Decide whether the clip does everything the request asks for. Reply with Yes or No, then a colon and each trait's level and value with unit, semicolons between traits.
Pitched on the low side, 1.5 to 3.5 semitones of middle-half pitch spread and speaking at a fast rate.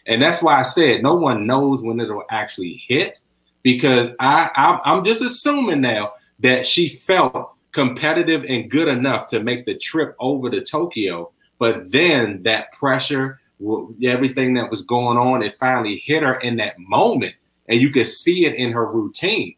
No: low, 125 Hz; average, 3.0 semitones; average, 175 wpm